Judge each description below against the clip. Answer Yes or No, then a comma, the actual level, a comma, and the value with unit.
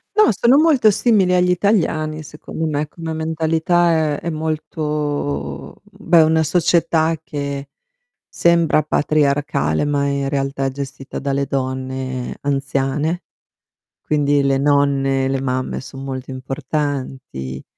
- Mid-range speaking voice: Yes, medium, 145 Hz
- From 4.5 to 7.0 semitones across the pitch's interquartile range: No, average, 2.9 semitones